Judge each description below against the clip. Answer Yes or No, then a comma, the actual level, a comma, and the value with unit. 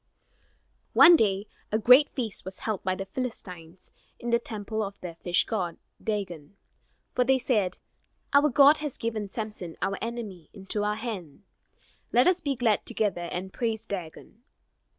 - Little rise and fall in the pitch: No, average, 4.1 semitones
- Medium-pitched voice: No, high, 210 Hz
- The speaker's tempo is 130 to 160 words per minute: Yes, average, 155 wpm